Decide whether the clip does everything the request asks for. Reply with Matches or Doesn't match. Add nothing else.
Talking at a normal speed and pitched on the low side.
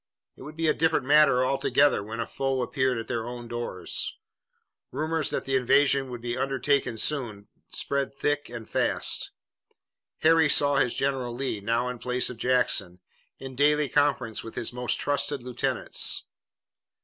Matches